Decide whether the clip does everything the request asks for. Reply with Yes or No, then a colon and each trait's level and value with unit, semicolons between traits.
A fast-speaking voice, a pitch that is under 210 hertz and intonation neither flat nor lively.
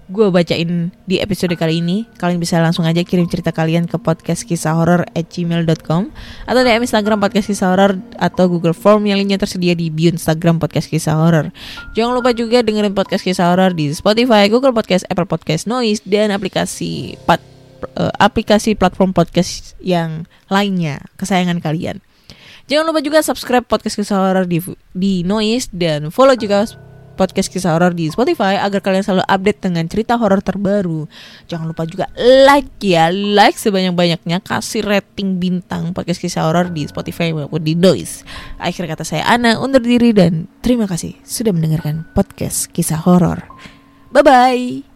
Yes: fast, 165 wpm; medium, 185 Hz; average, 3.9 semitones